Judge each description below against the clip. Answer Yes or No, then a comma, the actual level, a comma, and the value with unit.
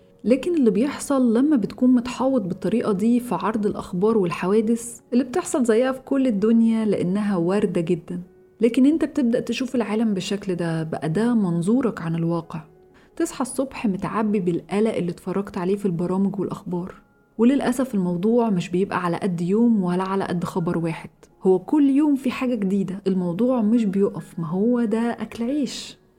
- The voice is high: Yes, high, 215 Hz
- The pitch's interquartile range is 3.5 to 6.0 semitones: Yes, average, 4.6 semitones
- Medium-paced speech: No, fast, 160 wpm